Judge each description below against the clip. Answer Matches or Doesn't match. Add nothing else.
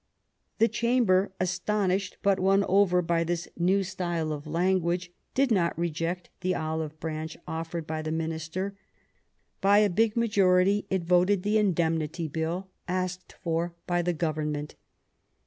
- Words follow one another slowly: Doesn't match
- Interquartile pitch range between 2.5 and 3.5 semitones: Matches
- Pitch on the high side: Doesn't match